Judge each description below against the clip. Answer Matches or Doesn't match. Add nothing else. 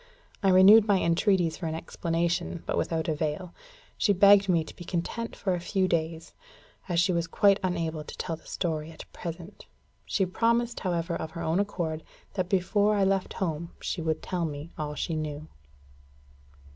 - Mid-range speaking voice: Matches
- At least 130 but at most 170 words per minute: Doesn't match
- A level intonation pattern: Doesn't match